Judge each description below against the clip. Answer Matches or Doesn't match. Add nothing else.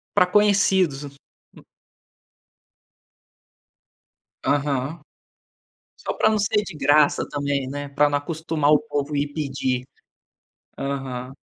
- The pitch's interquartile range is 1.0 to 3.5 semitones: Matches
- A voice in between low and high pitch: Matches